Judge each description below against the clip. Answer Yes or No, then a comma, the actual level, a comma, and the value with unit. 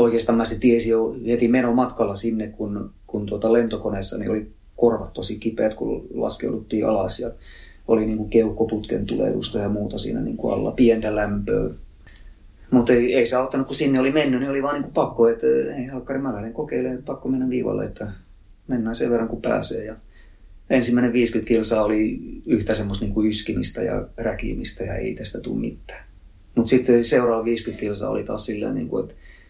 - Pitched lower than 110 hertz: No, low, 115 Hz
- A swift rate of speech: Yes, fast, 180 wpm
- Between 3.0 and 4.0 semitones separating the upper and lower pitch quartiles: No, narrow, 2.5 semitones